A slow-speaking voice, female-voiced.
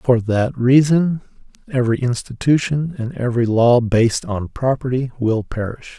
No: slow, 130 wpm; male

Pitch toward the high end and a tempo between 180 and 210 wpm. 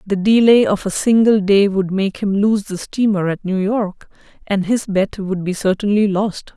Yes: high, 200 Hz; average, 200 wpm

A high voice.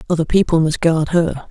No: medium, 165 Hz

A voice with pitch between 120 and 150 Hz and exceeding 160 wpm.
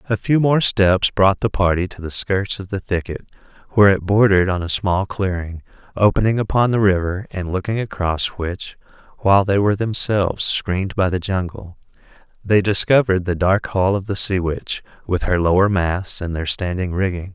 No: very low, 95 Hz; average, 175 wpm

